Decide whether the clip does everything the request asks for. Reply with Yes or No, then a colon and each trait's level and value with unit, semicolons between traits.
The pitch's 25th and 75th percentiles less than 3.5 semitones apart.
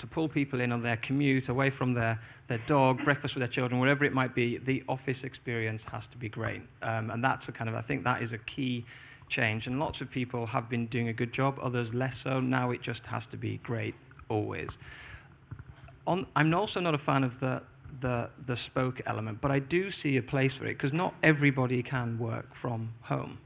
Yes: narrow, 2.4 semitones